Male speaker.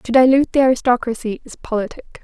No: female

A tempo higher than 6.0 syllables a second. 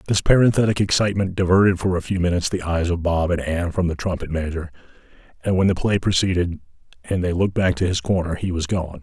Yes: 6.5 syllables/s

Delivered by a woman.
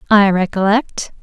Yes: female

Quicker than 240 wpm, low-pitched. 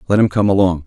Yes: fast, 275 wpm; very low, 95 Hz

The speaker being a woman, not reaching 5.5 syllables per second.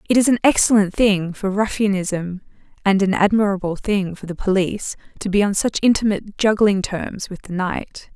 Yes: female; 5.2 syllables/s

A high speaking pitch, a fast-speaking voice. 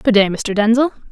Yes: high, 225 Hz; fast, 215 wpm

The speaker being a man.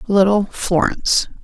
No: female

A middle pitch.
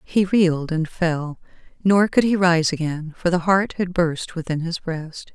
Yes: medium, 170 Hz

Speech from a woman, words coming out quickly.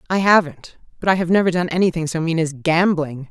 Yes: female; fast, 220 wpm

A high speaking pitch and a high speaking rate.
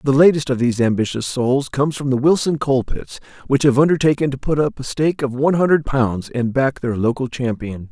No: low, 135 Hz; fast, 220 wpm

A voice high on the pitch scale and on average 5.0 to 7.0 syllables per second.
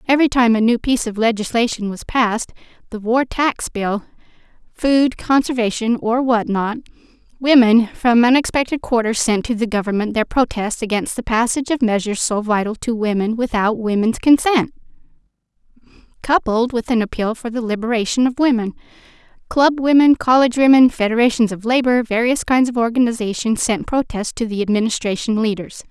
Yes: high, 235 Hz; 5.5 syllables/s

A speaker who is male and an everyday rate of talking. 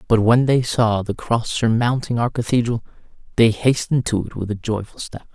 Yes: male; average, 190 wpm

